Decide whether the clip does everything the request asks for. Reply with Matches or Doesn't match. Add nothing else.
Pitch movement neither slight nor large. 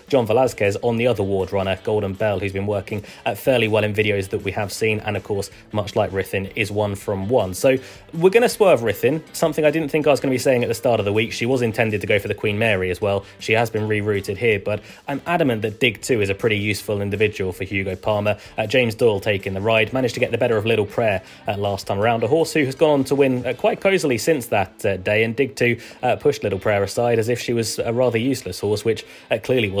Matches